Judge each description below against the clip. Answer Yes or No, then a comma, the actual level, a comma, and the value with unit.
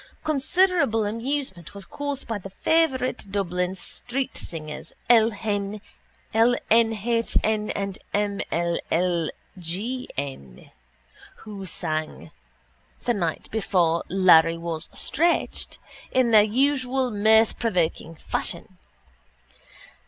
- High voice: Yes, high, 210 Hz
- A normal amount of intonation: No, wide, 5.7 semitones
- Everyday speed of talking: No, slow, 95 wpm